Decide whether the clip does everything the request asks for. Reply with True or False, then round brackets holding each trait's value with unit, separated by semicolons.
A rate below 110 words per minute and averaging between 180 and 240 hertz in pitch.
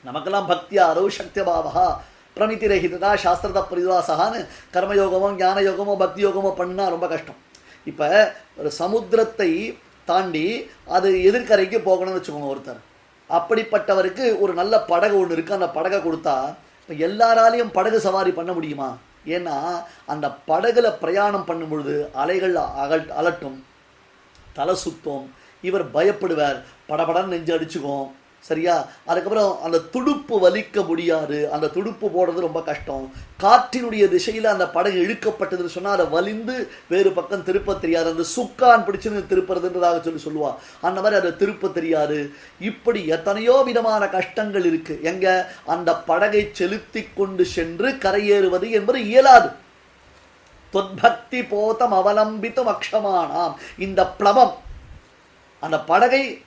False (115 wpm; 190 Hz)